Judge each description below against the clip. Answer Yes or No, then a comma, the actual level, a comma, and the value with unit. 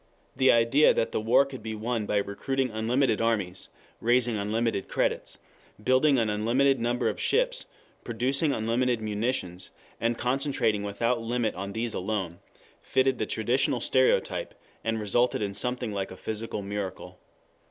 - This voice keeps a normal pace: Yes, average, 145 wpm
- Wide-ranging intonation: No, average, 3.3 semitones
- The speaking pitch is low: Yes, low, 115 Hz